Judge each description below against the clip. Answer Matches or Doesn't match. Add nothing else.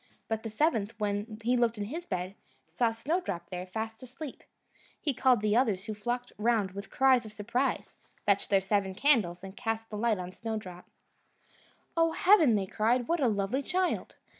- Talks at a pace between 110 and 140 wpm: Doesn't match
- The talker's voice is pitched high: Matches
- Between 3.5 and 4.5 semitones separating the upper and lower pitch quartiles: Matches